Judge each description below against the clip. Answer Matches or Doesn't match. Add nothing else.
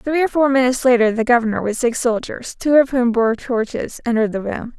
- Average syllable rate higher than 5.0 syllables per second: Matches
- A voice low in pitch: Doesn't match